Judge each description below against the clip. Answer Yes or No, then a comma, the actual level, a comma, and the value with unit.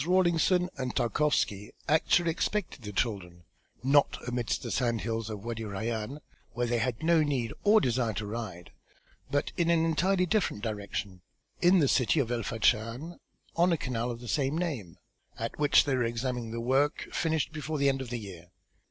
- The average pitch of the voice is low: Yes, low, 125 Hz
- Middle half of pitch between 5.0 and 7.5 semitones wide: Yes, wide, 5.6 semitones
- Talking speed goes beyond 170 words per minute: Yes, average, 180 wpm